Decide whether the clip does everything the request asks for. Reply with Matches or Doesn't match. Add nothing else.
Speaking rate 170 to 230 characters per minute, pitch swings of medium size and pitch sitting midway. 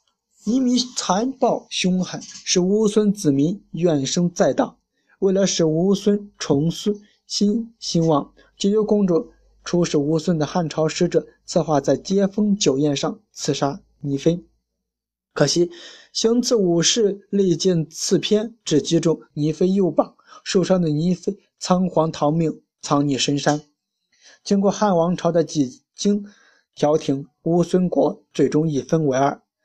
Matches